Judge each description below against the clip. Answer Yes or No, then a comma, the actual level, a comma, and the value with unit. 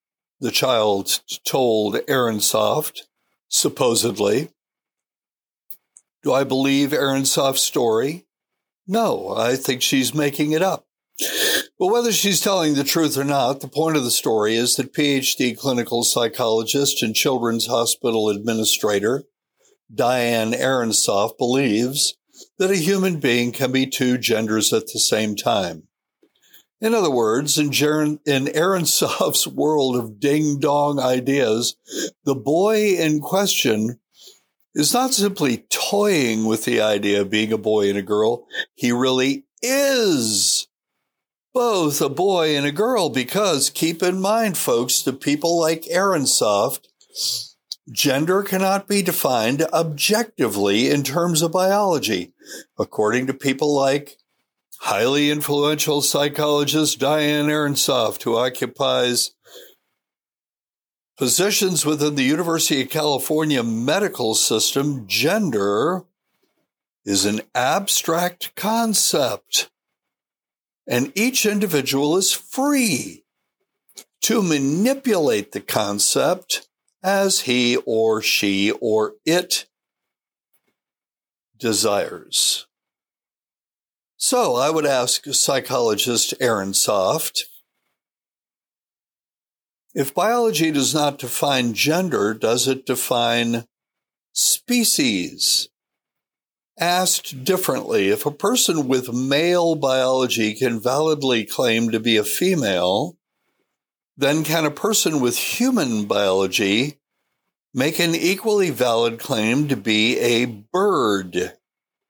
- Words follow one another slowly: Yes, slow, 105 wpm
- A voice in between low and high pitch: Yes, medium, 145 Hz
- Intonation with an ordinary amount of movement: No, wide, 6.6 semitones